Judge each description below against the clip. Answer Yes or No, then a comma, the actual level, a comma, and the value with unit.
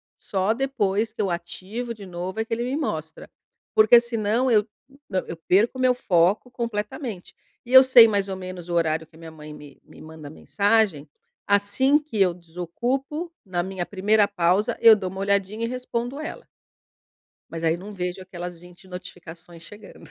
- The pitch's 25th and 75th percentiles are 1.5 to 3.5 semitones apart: No, average, 4.7 semitones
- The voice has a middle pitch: No, high, 200 Hz